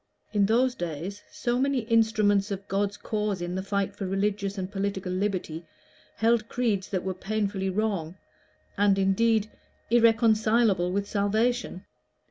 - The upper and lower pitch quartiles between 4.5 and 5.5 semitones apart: No, narrow, 2.4 semitones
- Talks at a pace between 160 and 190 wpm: No, slow, 135 wpm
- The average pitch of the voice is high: Yes, high, 200 Hz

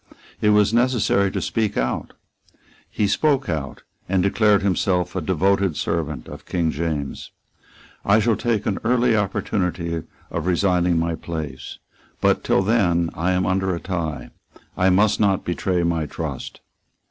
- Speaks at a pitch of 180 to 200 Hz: No, very low, 95 Hz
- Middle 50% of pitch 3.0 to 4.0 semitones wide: Yes, average, 3.5 semitones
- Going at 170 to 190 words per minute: No, average, 145 wpm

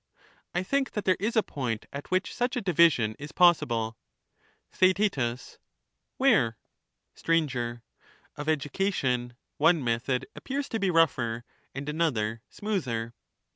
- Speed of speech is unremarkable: No, slow, 125 wpm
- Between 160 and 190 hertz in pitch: No, medium, 150 Hz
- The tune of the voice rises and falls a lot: Yes, wide, 7.8 semitones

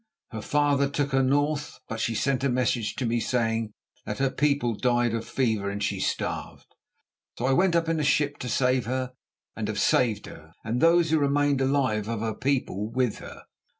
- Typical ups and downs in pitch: Yes, average, 3.9 semitones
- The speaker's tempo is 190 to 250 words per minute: Yes, average, 200 wpm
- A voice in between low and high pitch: No, low, 130 Hz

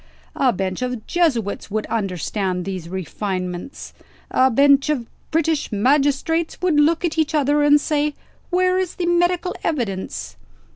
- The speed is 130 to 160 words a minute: Yes, average, 140 wpm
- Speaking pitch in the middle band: No, very high, 280 Hz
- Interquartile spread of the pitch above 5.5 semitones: Yes, wide, 7.9 semitones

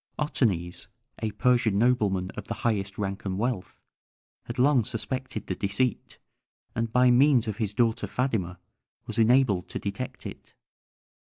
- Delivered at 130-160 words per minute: Yes, average, 145 wpm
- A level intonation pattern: No, average, 4.1 semitones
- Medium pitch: No, low, 115 Hz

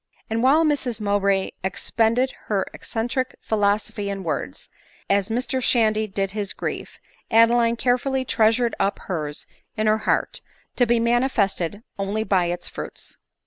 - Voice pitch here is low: No, high, 220 Hz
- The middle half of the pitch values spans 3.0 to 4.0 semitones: Yes, average, 3.4 semitones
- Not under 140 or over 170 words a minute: Yes, average, 145 wpm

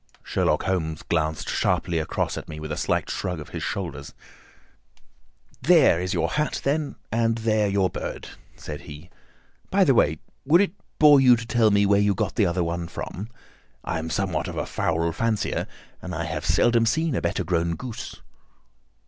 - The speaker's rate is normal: Yes, average, 180 wpm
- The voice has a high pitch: No, very low, 95 Hz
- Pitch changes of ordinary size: No, wide, 5.9 semitones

